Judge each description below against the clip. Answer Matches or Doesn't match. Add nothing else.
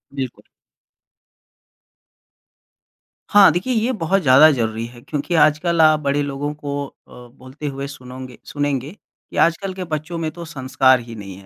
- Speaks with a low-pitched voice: Doesn't match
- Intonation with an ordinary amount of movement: Matches